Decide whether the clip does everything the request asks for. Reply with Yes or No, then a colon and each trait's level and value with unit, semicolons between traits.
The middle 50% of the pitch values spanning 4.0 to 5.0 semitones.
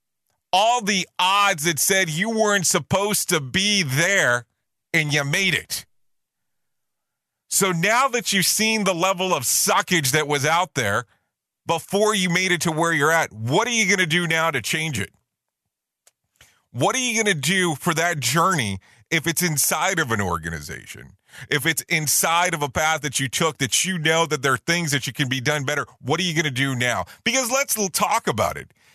Yes: average, 4.6 semitones